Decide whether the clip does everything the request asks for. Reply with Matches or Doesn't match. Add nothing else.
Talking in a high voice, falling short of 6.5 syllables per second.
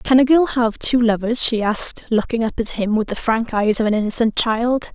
Matches